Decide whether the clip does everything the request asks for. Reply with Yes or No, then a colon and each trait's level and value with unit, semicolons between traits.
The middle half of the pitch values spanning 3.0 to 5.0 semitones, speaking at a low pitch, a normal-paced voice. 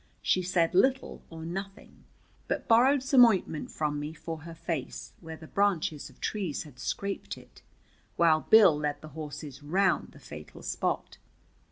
No: average, 4.4 semitones; medium, 165 Hz; average, 160 wpm